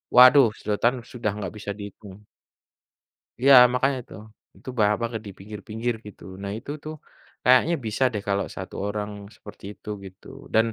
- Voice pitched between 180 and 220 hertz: No, low, 105 Hz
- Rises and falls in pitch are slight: No, average, 3.5 semitones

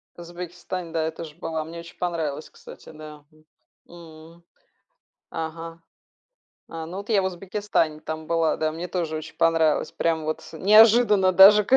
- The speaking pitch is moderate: Yes, medium, 165 Hz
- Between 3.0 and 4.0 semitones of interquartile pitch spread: No, narrow, 2.5 semitones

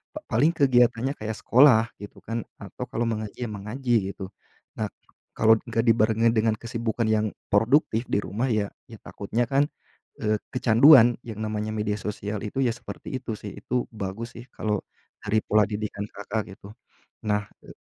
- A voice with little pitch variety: Yes, narrow, 2.1 semitones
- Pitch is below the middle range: Yes, low, 110 Hz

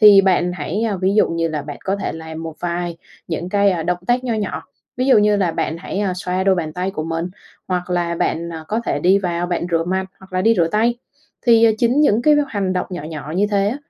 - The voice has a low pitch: No, medium, 185 Hz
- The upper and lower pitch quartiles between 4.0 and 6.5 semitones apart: No, average, 3.5 semitones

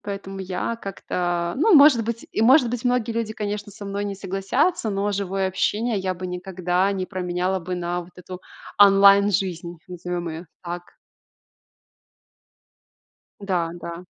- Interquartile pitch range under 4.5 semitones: Yes, narrow, 2.5 semitones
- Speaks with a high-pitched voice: Yes, high, 195 Hz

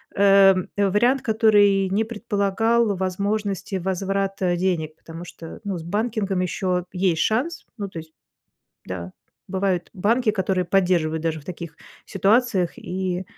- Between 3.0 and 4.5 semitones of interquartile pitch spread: No, narrow, 2.6 semitones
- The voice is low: No, high, 195 Hz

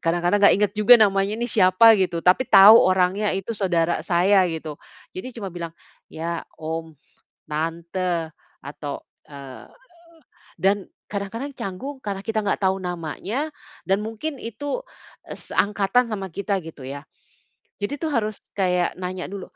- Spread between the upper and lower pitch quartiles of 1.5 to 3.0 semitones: No, average, 3.7 semitones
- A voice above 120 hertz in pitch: Yes, high, 190 Hz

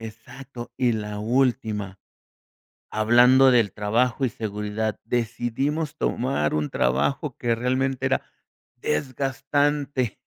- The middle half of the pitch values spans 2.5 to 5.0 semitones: Yes, average, 3.6 semitones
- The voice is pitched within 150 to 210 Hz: No, low, 120 Hz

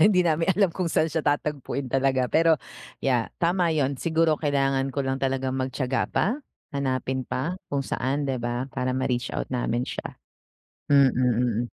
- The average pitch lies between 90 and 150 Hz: Yes, low, 135 Hz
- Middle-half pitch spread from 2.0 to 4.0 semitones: Yes, average, 3.2 semitones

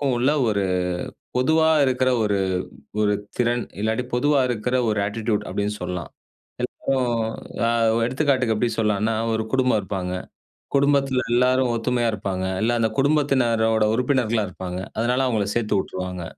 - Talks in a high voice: No, low, 115 Hz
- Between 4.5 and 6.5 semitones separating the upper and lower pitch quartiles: No, average, 3.4 semitones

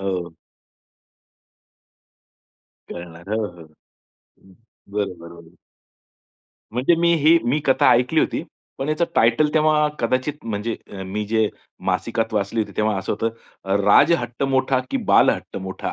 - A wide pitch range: Yes, wide, 5.9 semitones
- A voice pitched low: Yes, low, 115 Hz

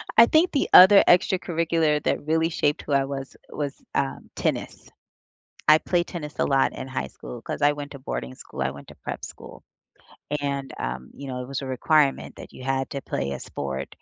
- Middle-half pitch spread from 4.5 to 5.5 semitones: No, average, 3.4 semitones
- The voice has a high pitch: No, medium, 140 Hz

